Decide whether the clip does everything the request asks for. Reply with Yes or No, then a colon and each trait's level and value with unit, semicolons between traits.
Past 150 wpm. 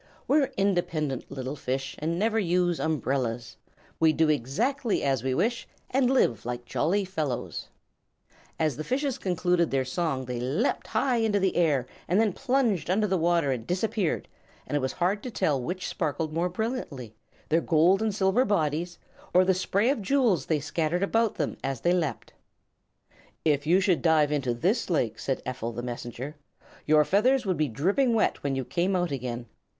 Yes: average, 175 wpm